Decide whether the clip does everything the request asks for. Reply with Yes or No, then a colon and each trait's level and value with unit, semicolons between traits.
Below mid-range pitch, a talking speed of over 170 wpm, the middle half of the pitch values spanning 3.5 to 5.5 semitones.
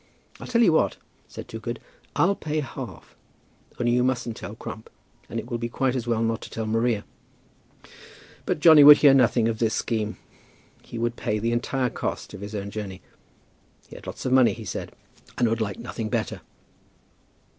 No: low, 120 Hz; average, 190 wpm; average, 2.8 semitones